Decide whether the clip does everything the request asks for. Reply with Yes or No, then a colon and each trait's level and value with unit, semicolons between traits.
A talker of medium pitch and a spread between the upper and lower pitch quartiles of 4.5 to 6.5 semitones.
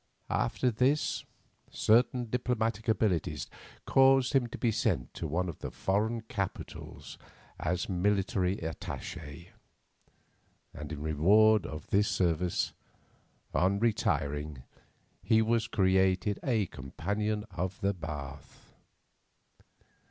No: very low, 95 Hz; average, 5.2 semitones